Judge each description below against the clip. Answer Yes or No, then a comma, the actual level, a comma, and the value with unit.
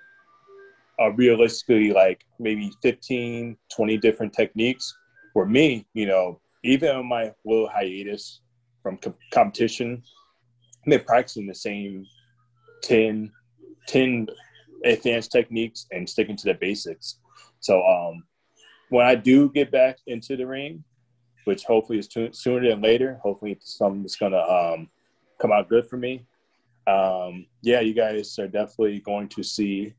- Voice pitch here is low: Yes, low, 115 Hz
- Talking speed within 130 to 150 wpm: Yes, average, 140 wpm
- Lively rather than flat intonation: No, average, 3.0 semitones